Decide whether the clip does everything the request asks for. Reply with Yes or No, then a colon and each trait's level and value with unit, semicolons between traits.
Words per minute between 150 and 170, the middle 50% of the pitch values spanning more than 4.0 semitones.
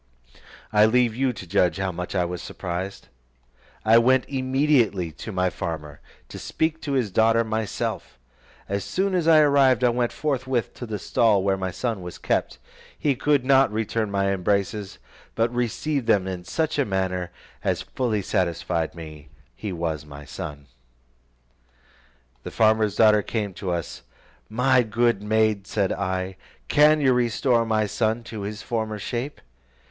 Yes: average, 160 wpm; average, 4.8 semitones